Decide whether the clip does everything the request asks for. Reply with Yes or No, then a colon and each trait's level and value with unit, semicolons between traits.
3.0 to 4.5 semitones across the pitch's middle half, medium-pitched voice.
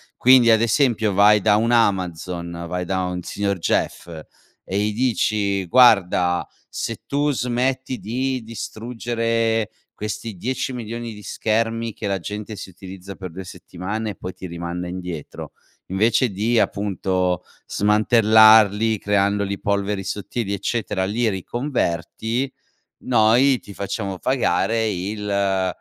No: average, 3.3 semitones; low, 105 Hz